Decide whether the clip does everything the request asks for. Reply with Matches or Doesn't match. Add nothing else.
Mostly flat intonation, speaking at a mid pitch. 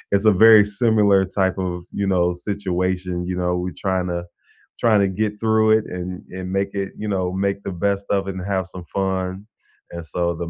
Doesn't match